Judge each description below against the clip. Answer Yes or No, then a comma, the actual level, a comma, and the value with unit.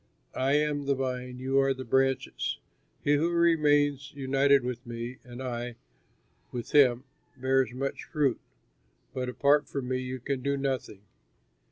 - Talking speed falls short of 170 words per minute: Yes, average, 150 wpm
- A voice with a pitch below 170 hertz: Yes, low, 135 Hz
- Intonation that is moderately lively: No, narrow, 1.9 semitones